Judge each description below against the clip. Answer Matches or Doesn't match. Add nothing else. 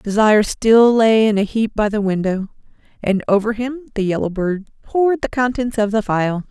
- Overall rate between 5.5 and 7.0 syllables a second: Doesn't match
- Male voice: Doesn't match